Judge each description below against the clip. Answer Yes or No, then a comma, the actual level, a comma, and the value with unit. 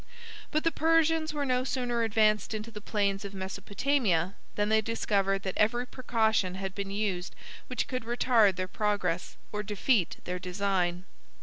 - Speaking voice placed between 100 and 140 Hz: No, high, 210 Hz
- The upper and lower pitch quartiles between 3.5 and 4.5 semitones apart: Yes, average, 3.8 semitones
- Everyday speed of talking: Yes, average, 160 wpm